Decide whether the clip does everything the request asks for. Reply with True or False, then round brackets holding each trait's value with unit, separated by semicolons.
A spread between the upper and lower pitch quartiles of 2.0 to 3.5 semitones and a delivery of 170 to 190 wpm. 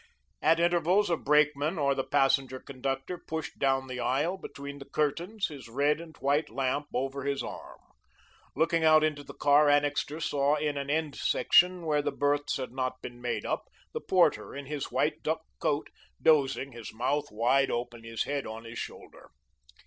True (2.5 semitones; 180 wpm)